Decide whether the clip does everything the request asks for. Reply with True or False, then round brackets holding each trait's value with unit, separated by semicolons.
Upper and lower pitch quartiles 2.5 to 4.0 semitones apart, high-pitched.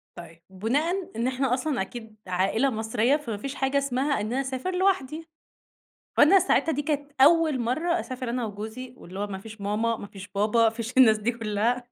False (4.5 semitones; 245 Hz)